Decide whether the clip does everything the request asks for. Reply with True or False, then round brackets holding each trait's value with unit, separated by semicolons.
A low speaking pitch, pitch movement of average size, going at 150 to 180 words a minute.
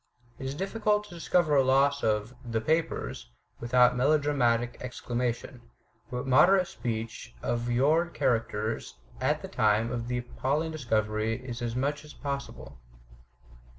False (125 Hz; 3.9 semitones; 140 wpm)